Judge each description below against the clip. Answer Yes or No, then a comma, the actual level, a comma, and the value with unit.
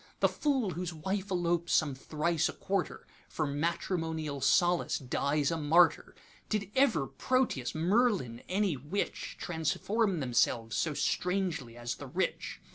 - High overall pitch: No, medium, 170 Hz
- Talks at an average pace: No, slow, 120 wpm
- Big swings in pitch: No, average, 4.8 semitones